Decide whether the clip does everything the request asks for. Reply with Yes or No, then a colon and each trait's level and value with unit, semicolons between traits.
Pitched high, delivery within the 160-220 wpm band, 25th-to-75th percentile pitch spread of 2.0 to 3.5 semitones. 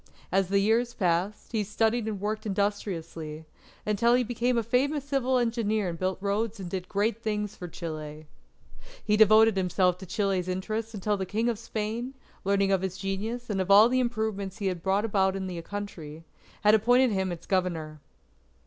Yes: high, 205 Hz; average, 180 wpm; average, 3.1 semitones